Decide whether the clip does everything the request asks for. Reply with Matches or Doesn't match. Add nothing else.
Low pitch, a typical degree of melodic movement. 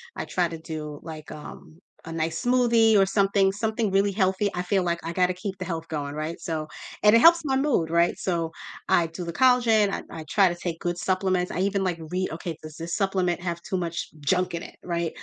Doesn't match